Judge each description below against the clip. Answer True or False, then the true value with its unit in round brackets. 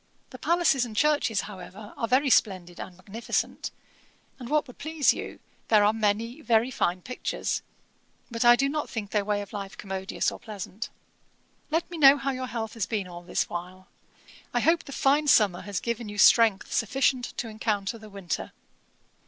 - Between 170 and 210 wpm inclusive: True (180 wpm)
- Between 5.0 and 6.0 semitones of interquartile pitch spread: False (4.5 semitones)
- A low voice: False (225 Hz)